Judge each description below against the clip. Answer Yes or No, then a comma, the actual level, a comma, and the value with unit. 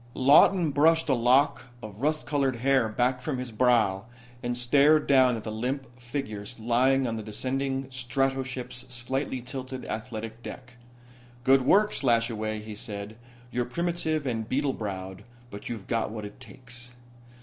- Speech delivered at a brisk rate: No, average, 150 wpm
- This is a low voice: Yes, low, 125 Hz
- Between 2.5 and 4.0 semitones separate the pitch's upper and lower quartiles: Yes, average, 3.2 semitones